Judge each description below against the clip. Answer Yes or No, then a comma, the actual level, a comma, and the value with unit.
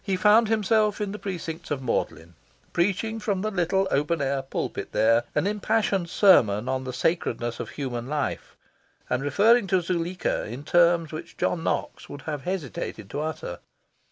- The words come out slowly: No, average, 165 wpm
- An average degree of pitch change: No, wide, 6.5 semitones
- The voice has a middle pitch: Yes, medium, 170 Hz